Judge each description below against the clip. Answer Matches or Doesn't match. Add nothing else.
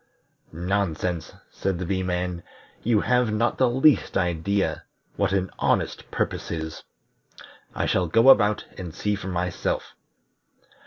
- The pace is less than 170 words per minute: Matches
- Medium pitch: Doesn't match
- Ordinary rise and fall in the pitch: Matches